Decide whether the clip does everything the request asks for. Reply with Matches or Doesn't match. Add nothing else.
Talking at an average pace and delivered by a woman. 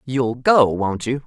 Matches